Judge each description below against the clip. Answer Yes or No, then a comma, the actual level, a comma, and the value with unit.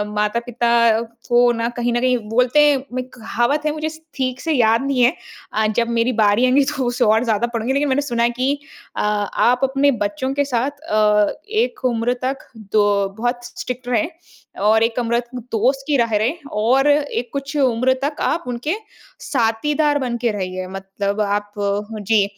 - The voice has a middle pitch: No, high, 240 Hz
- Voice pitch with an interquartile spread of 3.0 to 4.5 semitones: Yes, average, 3.3 semitones